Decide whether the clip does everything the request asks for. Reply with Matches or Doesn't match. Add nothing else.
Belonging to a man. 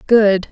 Doesn't match